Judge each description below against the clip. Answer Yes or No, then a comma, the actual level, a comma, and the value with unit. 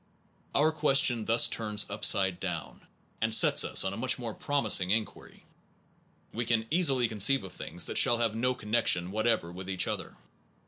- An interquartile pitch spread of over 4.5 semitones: No, average, 4.1 semitones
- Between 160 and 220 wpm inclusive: Yes, average, 170 wpm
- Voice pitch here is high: No, low, 110 Hz